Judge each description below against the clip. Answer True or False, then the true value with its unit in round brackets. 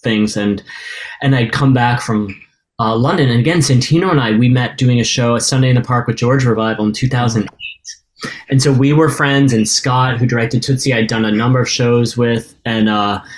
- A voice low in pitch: True (120 Hz)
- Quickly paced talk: True (215 wpm)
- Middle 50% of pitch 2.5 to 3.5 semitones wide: True (2.8 semitones)